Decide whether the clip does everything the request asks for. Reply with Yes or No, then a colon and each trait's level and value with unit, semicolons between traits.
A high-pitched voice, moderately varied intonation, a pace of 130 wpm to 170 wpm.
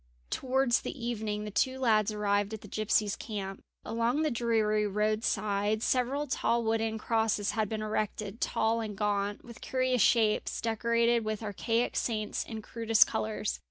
No: high, 220 Hz; narrow, 1.8 semitones; average, 155 wpm